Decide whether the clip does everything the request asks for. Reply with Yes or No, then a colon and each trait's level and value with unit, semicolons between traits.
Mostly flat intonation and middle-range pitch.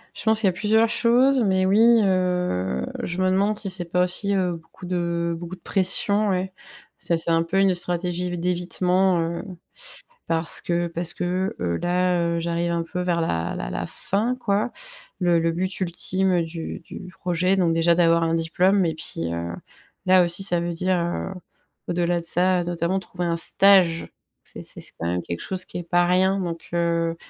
Yes: narrow, 2.0 semitones; medium, 175 Hz